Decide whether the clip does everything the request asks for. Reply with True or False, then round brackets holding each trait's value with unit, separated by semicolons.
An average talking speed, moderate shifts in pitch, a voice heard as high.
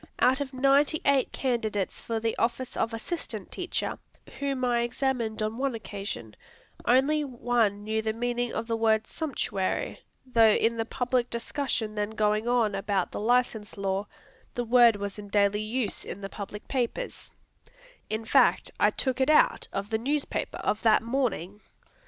True (165 wpm; 3.3 semitones; 230 Hz)